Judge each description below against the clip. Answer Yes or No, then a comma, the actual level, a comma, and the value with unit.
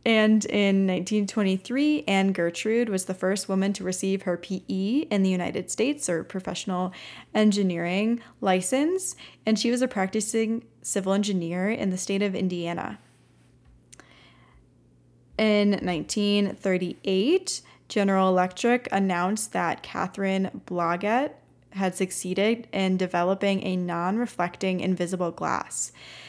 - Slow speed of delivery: Yes, slow, 110 wpm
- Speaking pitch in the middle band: No, high, 195 Hz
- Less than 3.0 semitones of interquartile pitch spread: Yes, narrow, 2.6 semitones